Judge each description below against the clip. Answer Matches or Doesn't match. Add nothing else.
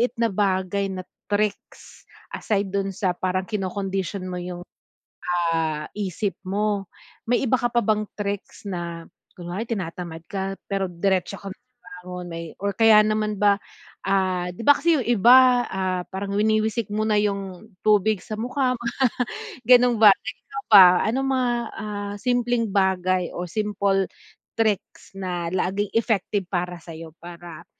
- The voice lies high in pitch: Matches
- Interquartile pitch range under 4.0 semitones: Matches